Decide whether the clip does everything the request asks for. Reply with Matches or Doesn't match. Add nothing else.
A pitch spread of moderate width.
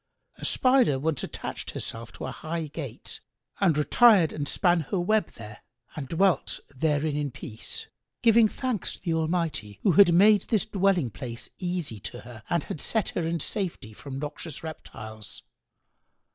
Doesn't match